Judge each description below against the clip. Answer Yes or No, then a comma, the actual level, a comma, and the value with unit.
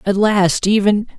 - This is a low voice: No, high, 200 Hz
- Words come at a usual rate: Yes, average, 150 wpm